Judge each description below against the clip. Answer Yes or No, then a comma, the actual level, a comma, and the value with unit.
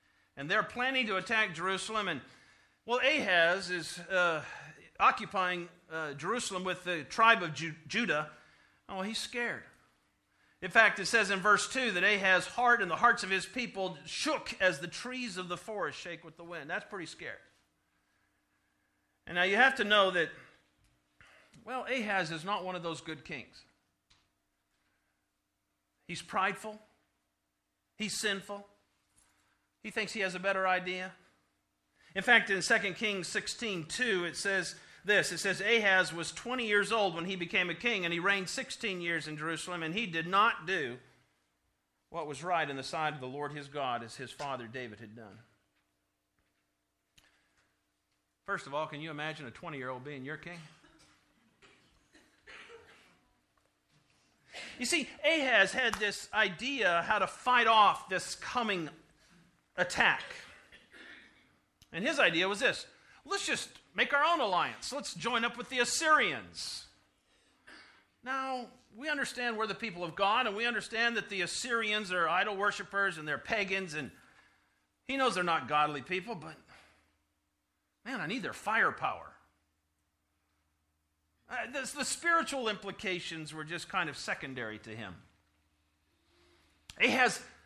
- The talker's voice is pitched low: No, medium, 185 Hz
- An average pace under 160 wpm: Yes, average, 150 wpm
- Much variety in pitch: Yes, wide, 7.1 semitones